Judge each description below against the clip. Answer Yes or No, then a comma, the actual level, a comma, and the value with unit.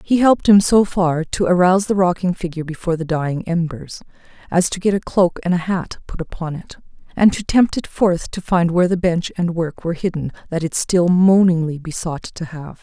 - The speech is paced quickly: Yes, fast, 210 wpm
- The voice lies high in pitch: No, medium, 175 Hz